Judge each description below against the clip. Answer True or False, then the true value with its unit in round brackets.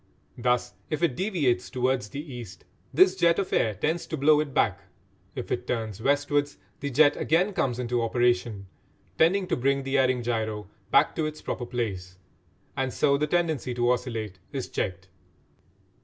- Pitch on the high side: False (130 Hz)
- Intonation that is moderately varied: True (4.4 semitones)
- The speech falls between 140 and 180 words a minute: True (170 wpm)